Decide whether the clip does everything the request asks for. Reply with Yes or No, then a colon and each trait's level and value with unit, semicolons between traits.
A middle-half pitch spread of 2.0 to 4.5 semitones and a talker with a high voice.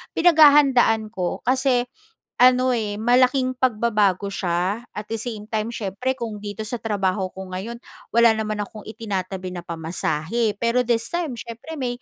Yes: average, 3.8 semitones; high, 220 Hz